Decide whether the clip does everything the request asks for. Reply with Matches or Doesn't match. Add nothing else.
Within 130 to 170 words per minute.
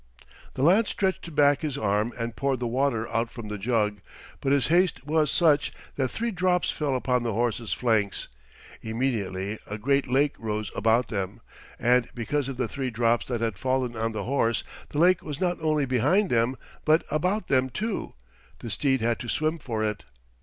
Doesn't match